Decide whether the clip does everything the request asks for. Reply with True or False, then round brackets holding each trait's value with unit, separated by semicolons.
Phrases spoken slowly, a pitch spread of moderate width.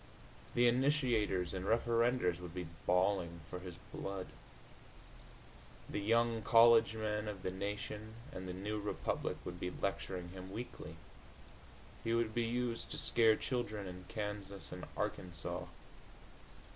True (130 wpm; 3.9 semitones)